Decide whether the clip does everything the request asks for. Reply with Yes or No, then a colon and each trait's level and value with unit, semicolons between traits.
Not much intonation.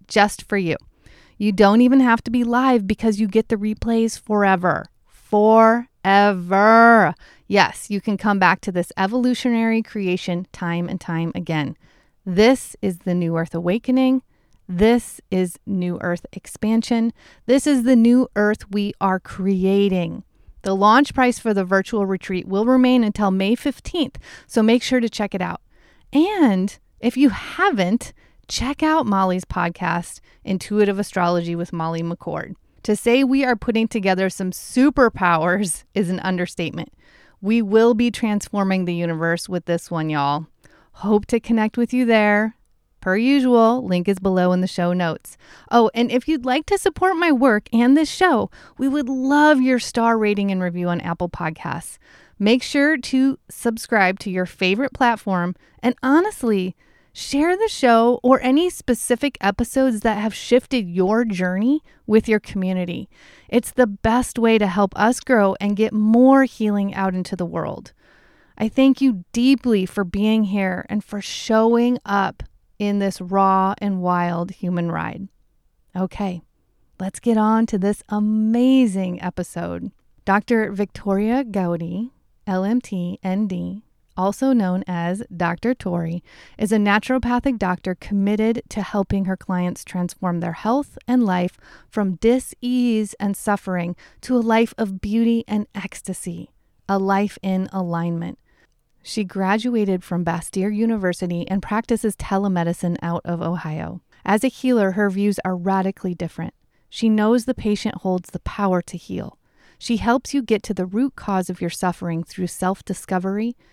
No: average, 4.3 semitones